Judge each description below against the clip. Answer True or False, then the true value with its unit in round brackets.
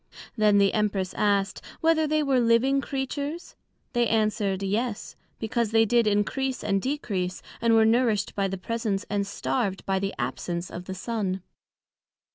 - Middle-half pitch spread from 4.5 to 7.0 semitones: False (3.6 semitones)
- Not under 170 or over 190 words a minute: False (155 wpm)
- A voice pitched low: False (215 Hz)